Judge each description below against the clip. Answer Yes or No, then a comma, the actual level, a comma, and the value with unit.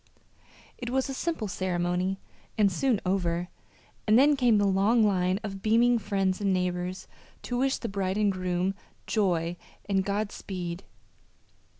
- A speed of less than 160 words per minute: Yes, average, 150 wpm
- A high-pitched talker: Yes, high, 195 Hz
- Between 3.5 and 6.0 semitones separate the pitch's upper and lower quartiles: No, average, 3.1 semitones